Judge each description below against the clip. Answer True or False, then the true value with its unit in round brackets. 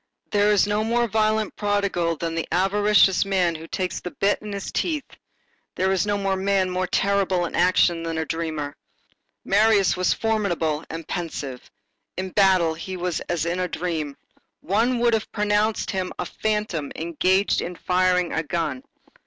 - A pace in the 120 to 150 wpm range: False (165 wpm)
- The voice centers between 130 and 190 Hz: True (185 Hz)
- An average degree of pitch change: True (3.5 semitones)